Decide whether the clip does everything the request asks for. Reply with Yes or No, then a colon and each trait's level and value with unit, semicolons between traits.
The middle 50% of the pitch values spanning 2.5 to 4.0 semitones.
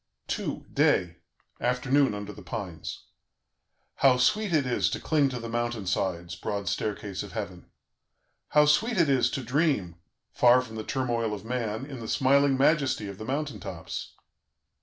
No: average, 5.0 semitones